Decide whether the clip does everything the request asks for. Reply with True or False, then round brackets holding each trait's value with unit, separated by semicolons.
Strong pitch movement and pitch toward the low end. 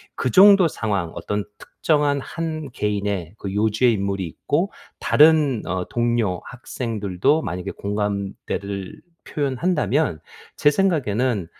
True (6.8 semitones; 110 Hz)